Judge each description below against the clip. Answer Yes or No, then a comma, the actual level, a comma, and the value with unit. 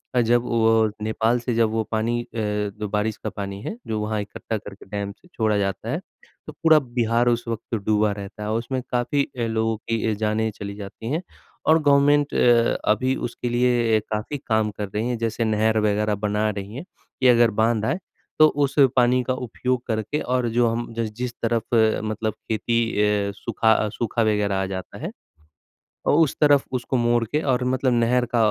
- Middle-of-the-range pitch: No, low, 115 Hz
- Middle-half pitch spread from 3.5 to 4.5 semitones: No, narrow, 2.4 semitones